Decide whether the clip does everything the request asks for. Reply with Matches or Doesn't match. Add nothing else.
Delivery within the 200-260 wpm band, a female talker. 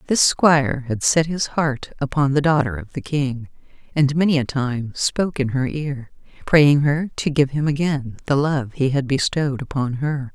Doesn't match